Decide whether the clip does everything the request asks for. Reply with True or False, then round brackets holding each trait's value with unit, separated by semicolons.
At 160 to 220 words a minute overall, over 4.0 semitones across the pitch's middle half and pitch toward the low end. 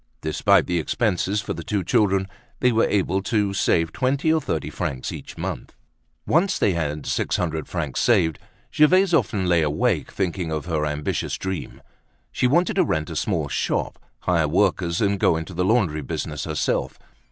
True (175 wpm; 4.9 semitones; 90 Hz)